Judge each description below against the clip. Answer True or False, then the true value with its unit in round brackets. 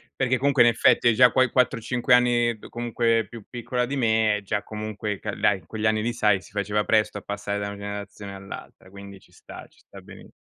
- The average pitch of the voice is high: False (110 Hz)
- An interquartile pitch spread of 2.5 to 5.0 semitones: True (2.8 semitones)